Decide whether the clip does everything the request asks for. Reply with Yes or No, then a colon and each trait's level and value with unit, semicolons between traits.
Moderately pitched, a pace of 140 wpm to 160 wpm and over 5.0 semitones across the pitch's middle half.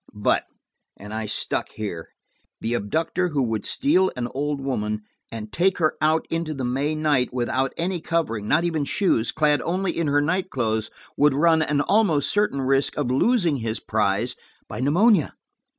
Yes: medium, 145 Hz; average, 155 wpm; wide, 5.5 semitones